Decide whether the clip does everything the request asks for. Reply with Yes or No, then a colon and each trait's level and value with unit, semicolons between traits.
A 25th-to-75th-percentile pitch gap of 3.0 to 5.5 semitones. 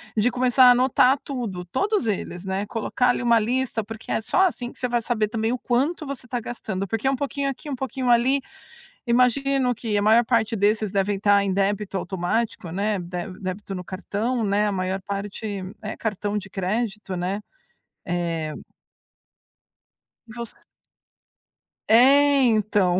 Yes: average, 4.0 semitones